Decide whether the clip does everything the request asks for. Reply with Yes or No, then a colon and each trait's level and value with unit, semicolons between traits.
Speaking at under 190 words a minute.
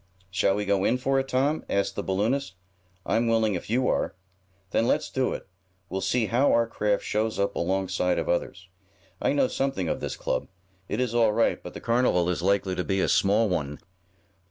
No: fast, 205 wpm